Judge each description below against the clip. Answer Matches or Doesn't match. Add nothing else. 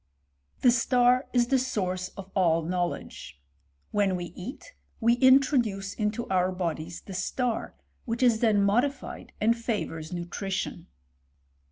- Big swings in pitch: Doesn't match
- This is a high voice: Matches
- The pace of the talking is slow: Matches